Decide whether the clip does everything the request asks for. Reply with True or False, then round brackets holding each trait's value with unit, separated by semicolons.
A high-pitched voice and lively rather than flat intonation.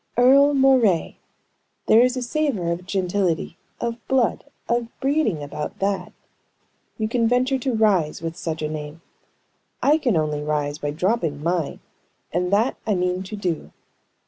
True (195 Hz; 6.9 semitones)